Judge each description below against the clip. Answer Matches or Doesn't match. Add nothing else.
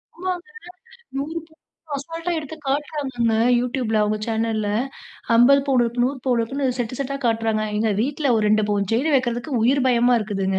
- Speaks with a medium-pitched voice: Doesn't match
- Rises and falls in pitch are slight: Doesn't match